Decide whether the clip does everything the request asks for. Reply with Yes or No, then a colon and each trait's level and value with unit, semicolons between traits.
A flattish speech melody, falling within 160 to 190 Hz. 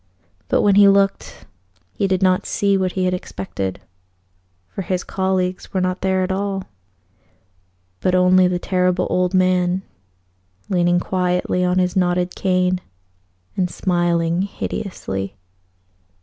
Yes: narrow, 0.9 semitones; medium, 185 Hz